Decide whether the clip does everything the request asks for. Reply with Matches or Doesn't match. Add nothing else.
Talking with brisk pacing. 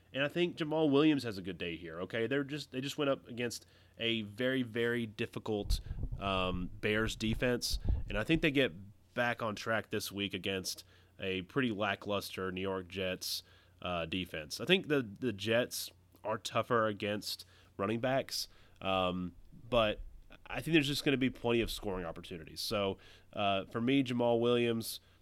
Doesn't match